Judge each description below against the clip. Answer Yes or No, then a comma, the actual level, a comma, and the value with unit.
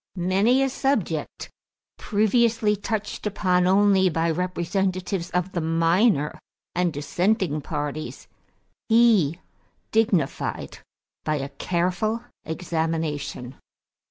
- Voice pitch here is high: No, medium, 180 Hz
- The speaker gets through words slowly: Yes, slow, 90 wpm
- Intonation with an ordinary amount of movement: Yes, average, 4.4 semitones